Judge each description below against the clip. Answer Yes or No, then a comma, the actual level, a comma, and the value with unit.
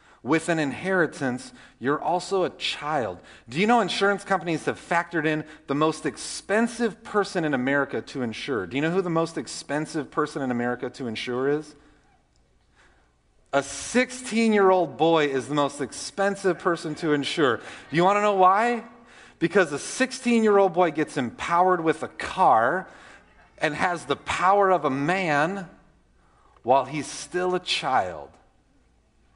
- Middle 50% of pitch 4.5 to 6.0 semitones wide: Yes, average, 5.2 semitones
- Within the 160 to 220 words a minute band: No, average, 150 wpm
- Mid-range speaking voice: Yes, medium, 165 Hz